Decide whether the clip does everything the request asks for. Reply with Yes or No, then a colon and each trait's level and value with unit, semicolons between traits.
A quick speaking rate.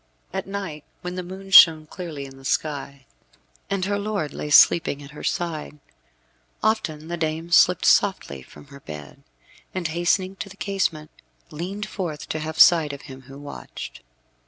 No: average, 165 wpm